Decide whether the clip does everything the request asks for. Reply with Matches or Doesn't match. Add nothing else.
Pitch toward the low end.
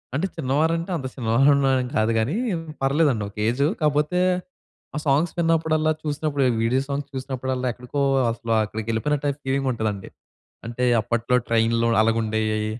Matches